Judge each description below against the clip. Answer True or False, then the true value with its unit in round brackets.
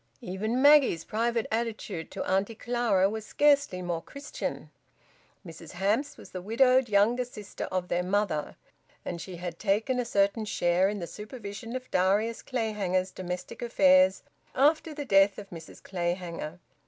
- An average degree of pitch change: True (4.4 semitones)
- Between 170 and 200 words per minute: False (150 wpm)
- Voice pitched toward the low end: False (205 Hz)